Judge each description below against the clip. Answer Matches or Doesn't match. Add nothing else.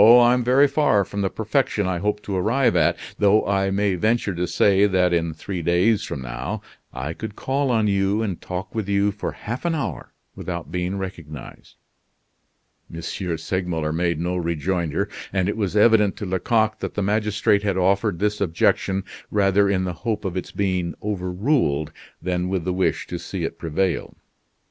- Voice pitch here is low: Matches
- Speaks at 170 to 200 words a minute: Matches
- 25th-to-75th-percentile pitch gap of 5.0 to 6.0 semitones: Doesn't match